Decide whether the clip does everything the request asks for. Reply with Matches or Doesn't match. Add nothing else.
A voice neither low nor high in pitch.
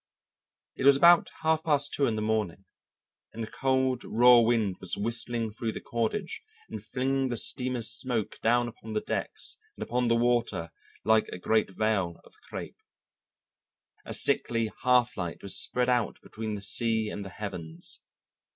Doesn't match